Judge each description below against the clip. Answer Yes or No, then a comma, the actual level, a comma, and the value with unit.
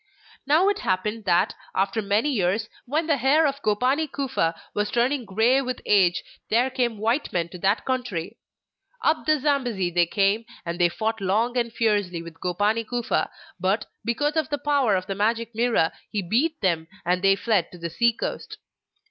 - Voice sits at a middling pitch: No, high, 220 Hz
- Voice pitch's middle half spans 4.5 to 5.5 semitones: Yes, average, 5.2 semitones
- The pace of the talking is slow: No, average, 180 wpm